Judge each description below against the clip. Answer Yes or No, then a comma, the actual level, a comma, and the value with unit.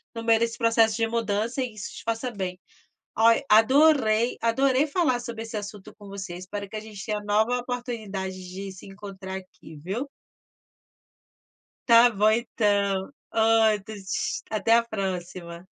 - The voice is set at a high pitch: Yes, high, 220 Hz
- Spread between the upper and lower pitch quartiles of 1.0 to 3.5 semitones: Yes, average, 2.8 semitones